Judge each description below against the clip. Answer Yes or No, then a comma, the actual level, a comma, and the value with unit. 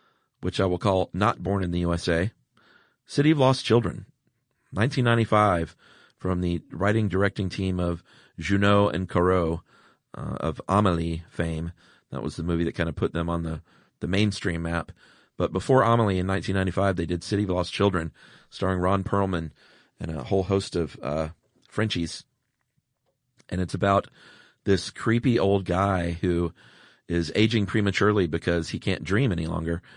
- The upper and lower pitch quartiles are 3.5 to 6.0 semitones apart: Yes, average, 3.8 semitones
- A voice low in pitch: Yes, very low, 95 Hz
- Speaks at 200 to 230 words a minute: No, average, 155 wpm